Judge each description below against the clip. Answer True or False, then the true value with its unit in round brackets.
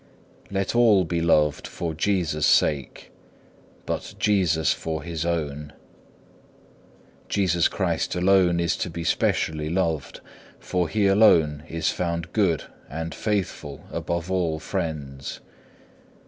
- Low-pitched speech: True (85 Hz)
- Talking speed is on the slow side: True (120 wpm)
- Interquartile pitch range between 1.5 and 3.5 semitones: True (3.0 semitones)